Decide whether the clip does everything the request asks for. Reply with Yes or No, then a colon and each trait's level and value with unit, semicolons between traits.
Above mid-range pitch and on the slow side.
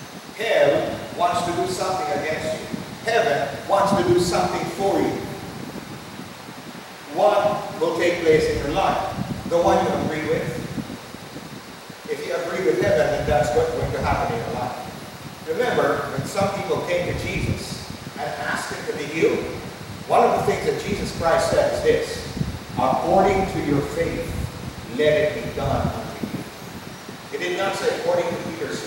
No: high, 195 Hz; average, 165 wpm